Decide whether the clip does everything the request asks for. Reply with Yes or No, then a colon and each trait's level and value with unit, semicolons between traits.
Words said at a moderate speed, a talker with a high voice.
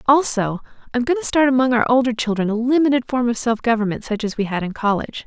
No: fast, 250 wpm; high, 240 Hz